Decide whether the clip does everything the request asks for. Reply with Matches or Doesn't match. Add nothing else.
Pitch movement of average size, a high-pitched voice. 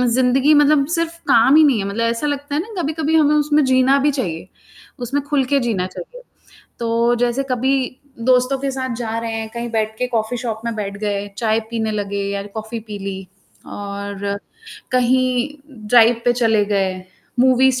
Matches